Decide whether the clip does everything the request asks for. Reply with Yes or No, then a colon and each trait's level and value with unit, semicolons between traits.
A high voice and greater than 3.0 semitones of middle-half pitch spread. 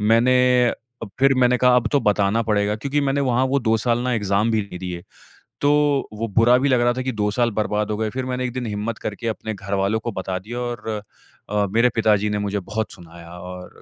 No: low, 115 Hz; average, 3.5 semitones